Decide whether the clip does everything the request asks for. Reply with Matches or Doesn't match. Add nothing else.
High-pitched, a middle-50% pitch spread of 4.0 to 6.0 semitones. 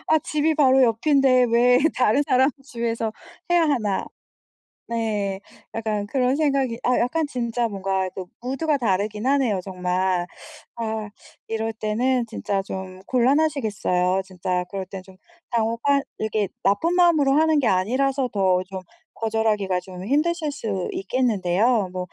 Matches